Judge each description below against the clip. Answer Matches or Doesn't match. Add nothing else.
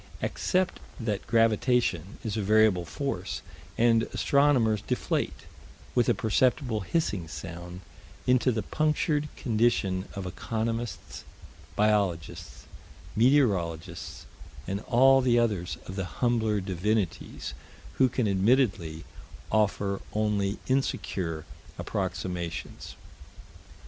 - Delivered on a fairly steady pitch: Doesn't match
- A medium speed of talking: Doesn't match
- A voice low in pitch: Matches